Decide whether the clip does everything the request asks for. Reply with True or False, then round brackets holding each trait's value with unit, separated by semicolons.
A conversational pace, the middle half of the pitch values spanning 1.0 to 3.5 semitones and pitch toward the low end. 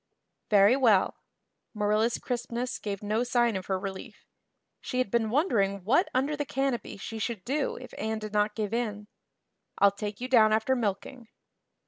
False (165 wpm; 3.2 semitones; 220 Hz)